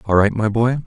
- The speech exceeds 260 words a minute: Yes, fast, 275 wpm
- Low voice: Yes, low, 115 Hz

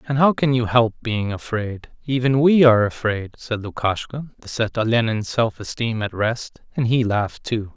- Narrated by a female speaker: No, male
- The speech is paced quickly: No, average, 185 wpm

